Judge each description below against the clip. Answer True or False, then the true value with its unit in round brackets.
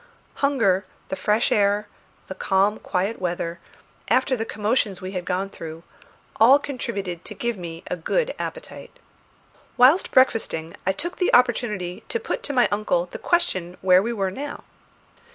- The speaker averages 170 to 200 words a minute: False (155 wpm)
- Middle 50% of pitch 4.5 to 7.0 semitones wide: True (5.5 semitones)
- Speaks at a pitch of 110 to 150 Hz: False (205 Hz)